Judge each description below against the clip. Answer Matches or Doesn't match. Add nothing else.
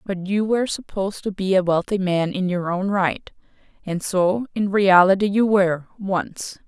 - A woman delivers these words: Matches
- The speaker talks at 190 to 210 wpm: Doesn't match